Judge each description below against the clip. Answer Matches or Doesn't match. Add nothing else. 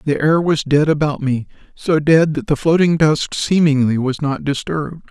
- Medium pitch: Matches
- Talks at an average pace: Matches